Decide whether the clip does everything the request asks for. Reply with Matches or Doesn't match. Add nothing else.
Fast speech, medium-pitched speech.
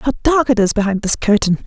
Doesn't match